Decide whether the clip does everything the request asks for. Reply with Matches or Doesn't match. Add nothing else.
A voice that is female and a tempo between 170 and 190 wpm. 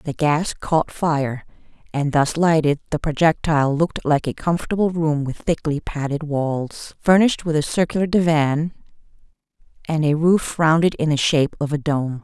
Doesn't match